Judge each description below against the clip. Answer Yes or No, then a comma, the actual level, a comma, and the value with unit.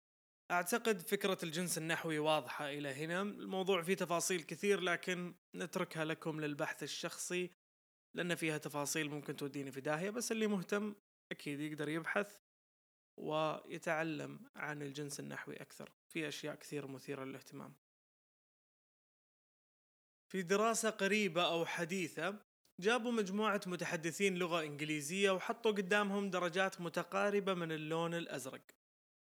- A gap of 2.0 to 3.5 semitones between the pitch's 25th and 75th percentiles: No, average, 4.2 semitones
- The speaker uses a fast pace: No, average, 115 wpm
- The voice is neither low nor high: Yes, medium, 170 Hz